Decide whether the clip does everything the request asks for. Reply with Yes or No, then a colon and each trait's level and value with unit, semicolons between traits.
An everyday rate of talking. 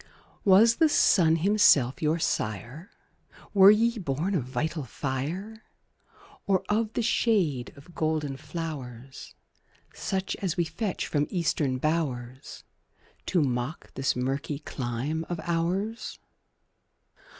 No: slow, 115 wpm